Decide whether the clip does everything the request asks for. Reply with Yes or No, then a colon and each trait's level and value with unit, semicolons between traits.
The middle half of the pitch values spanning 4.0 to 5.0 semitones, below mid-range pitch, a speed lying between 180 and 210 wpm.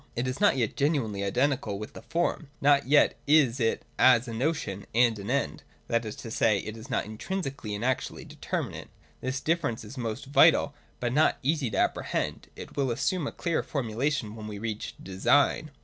Yes: average, 4.5 semitones; low, 125 Hz; average, 190 wpm